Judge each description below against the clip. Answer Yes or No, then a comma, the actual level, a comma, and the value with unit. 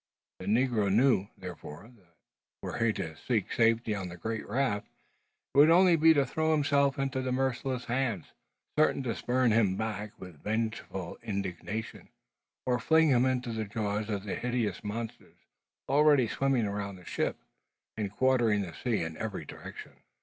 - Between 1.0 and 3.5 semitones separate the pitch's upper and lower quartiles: No, average, 4.3 semitones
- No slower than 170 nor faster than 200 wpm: No, average, 160 wpm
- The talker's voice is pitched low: Yes, low, 115 Hz